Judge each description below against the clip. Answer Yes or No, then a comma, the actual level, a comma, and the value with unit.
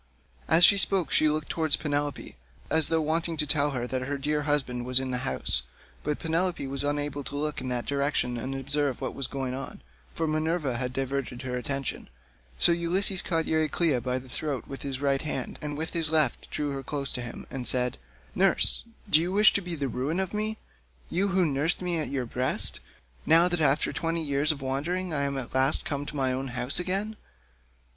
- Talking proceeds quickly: Yes, fast, 210 wpm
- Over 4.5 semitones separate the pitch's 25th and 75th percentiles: No, average, 3.5 semitones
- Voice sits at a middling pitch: Yes, medium, 145 Hz